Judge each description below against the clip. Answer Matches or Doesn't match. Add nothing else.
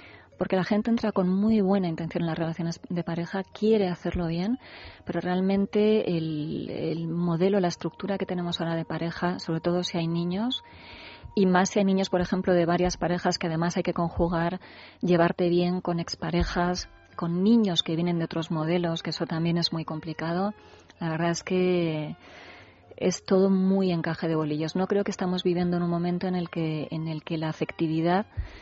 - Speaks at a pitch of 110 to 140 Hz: Doesn't match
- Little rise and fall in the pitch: Matches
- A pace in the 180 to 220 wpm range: Matches